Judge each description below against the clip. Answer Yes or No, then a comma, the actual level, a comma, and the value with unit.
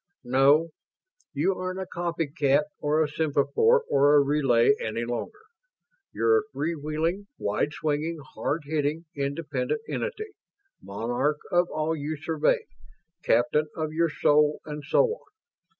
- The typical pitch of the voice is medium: Yes, medium, 150 Hz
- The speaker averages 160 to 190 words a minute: No, slow, 135 wpm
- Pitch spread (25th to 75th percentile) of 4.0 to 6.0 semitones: No, average, 2.9 semitones